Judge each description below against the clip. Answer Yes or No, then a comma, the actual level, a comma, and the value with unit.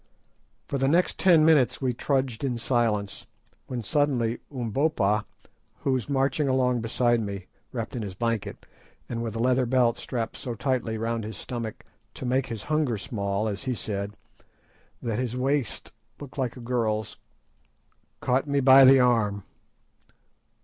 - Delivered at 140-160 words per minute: Yes, average, 155 wpm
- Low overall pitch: Yes, low, 120 Hz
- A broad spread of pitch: No, average, 3.0 semitones